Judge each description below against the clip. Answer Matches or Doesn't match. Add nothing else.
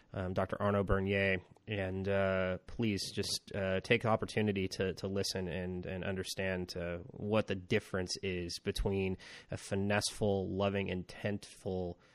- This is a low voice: Matches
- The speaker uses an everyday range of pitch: Doesn't match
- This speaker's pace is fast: Doesn't match